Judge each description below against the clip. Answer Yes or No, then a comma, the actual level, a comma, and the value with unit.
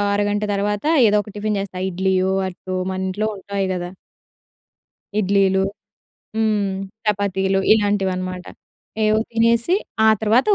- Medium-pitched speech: No, high, 200 Hz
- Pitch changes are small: Yes, narrow, 1.9 semitones